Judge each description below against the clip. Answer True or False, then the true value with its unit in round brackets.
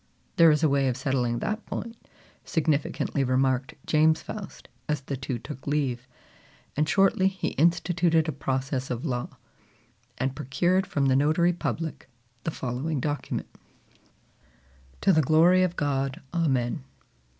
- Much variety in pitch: False (4.0 semitones)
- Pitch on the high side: False (145 Hz)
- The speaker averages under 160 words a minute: True (140 wpm)